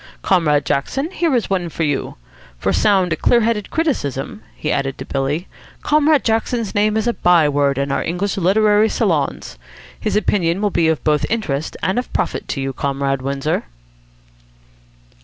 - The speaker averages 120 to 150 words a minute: No, average, 165 wpm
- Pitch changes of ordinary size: No, wide, 7.3 semitones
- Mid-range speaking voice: Yes, medium, 180 Hz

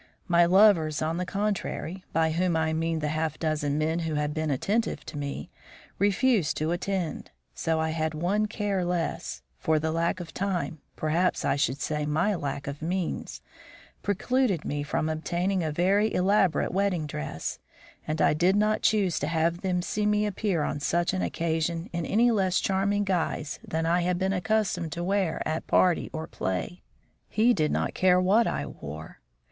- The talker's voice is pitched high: No, medium, 170 Hz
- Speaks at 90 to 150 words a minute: No, average, 180 wpm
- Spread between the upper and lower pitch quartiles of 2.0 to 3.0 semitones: No, average, 3.7 semitones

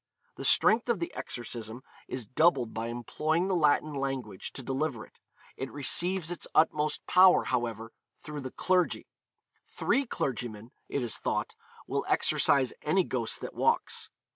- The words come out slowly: No, average, 145 wpm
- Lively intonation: Yes, wide, 5.7 semitones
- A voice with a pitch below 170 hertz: Yes, low, 135 Hz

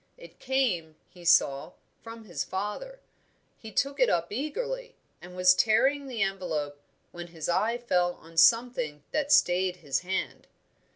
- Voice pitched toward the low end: No, high, 190 Hz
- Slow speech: No, average, 150 wpm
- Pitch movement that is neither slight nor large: No, wide, 6.9 semitones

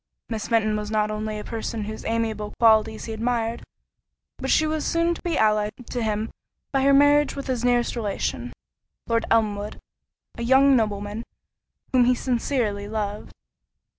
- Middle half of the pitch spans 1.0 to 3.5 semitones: Yes, average, 2.7 semitones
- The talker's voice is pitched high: Yes, high, 225 Hz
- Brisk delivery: No, average, 160 wpm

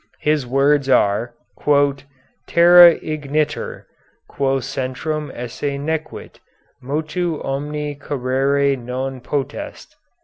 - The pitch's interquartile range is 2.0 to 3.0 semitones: Yes, narrow, 2.5 semitones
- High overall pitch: No, medium, 140 Hz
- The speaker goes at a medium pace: No, slow, 80 wpm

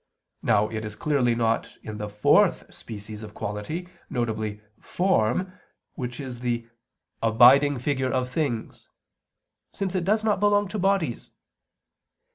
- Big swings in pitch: Yes, wide, 7.6 semitones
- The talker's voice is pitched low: Yes, low, 125 Hz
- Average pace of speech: No, slow, 130 wpm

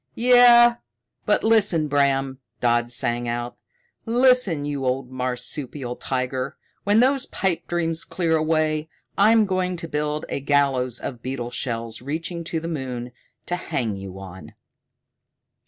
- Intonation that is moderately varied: No, wide, 5.8 semitones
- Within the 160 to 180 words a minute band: No, slow, 135 wpm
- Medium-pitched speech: Yes, medium, 145 Hz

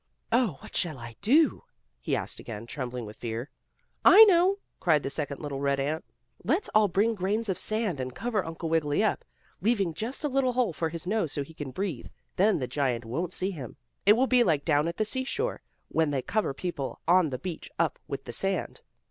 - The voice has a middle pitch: Yes, medium, 170 Hz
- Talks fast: Yes, fast, 210 wpm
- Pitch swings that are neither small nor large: No, wide, 7.6 semitones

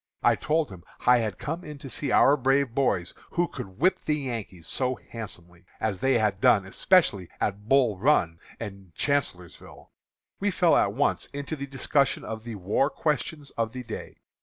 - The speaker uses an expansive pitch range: Yes, wide, 6.2 semitones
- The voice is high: No, low, 125 Hz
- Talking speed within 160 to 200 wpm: Yes, average, 180 wpm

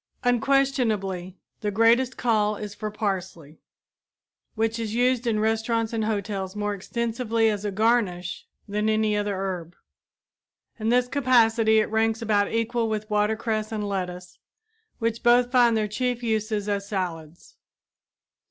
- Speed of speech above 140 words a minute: No, slow, 135 wpm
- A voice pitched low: No, high, 220 Hz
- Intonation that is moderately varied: No, narrow, 2.2 semitones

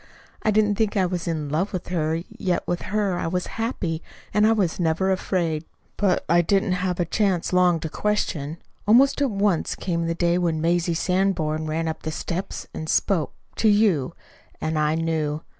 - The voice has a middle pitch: Yes, medium, 175 Hz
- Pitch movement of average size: Yes, average, 3.5 semitones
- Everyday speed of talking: Yes, average, 190 wpm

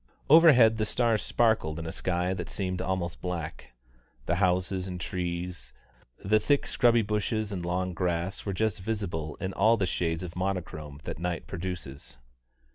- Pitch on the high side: No, very low, 90 Hz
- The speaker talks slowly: No, average, 160 wpm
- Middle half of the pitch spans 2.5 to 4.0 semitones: Yes, average, 3.5 semitones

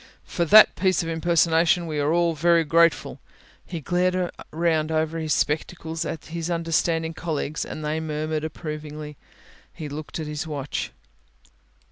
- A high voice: No, medium, 160 Hz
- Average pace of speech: Yes, average, 145 wpm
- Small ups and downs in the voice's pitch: Yes, narrow, 1.7 semitones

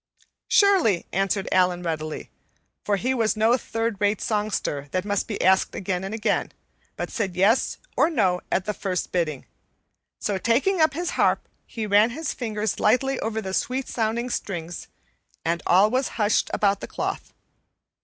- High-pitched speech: Yes, high, 210 Hz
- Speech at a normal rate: Yes, average, 165 wpm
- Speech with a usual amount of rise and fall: Yes, average, 3.8 semitones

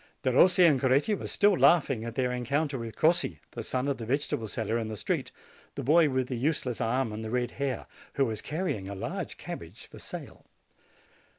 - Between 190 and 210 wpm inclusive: Yes, average, 200 wpm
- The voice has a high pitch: No, low, 130 Hz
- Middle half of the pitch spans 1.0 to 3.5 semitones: No, average, 4.2 semitones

